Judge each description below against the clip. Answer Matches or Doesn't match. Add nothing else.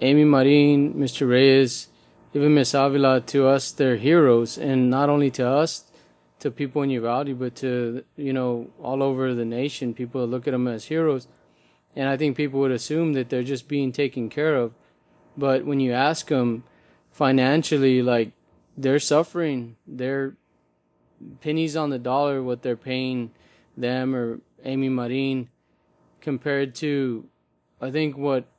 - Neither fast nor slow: Matches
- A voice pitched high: Doesn't match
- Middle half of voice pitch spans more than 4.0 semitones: Doesn't match